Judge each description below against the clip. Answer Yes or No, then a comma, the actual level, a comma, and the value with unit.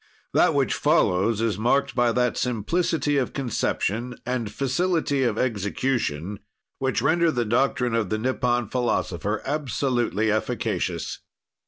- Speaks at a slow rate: Yes, slow, 125 wpm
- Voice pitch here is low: Yes, low, 120 Hz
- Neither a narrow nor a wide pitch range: Yes, average, 3.7 semitones